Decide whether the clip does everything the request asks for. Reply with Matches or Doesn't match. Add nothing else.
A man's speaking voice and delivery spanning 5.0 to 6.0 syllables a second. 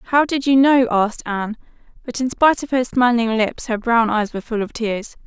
Doesn't match